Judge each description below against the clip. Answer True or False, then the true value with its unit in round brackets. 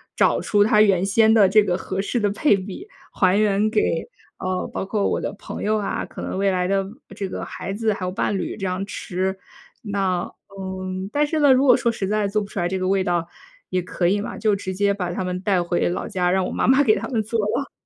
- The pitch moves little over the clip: True (2.3 semitones)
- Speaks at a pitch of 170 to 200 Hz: True (195 Hz)